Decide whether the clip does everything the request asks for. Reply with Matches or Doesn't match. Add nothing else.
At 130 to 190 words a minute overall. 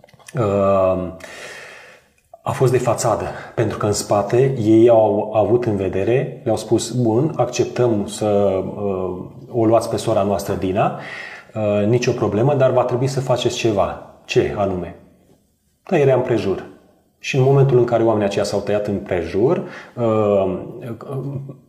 Matches